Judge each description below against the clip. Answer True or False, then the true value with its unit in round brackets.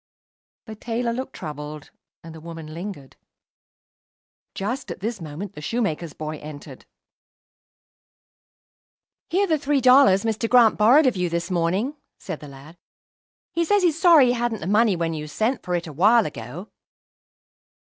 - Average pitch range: False (7.3 semitones)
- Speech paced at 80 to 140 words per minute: False (155 wpm)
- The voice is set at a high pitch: True (195 Hz)